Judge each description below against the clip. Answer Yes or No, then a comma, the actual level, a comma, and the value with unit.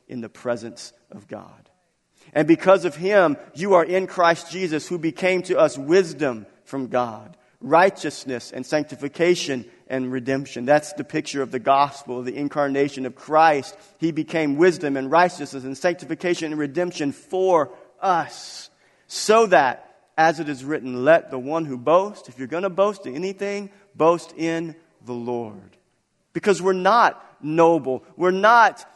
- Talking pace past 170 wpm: No, average, 155 wpm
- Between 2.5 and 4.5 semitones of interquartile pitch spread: No, average, 5.2 semitones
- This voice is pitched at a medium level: Yes, medium, 160 Hz